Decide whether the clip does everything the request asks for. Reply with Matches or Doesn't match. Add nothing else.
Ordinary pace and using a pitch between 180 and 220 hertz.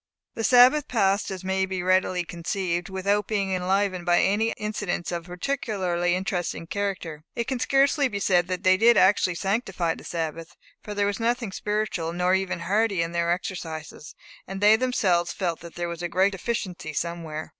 Matches